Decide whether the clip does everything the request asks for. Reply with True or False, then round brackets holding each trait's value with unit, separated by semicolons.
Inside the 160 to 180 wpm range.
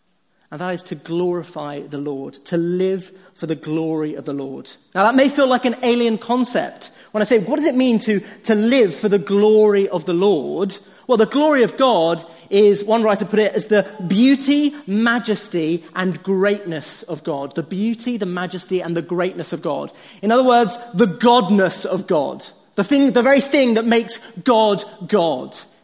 False (190 wpm)